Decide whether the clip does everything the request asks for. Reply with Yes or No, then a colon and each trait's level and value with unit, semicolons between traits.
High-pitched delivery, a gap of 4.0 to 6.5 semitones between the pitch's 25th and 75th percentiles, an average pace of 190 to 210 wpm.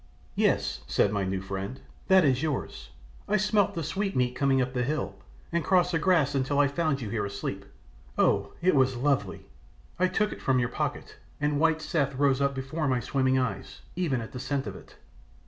No: medium, 140 Hz; average, 4.3 semitones; average, 200 wpm